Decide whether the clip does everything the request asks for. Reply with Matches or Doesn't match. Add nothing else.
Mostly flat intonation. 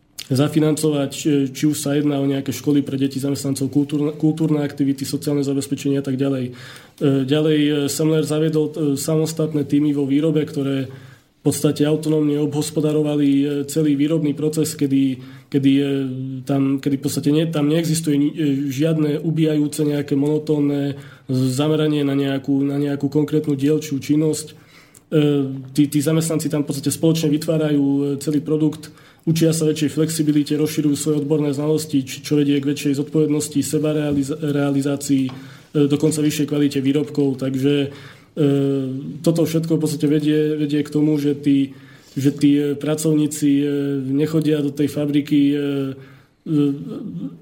Matches